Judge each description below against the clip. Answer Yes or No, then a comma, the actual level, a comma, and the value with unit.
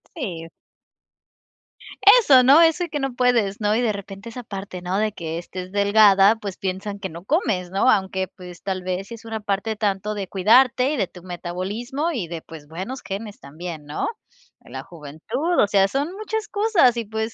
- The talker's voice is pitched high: Yes, high, 200 Hz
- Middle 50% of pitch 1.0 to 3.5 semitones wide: No, average, 4.8 semitones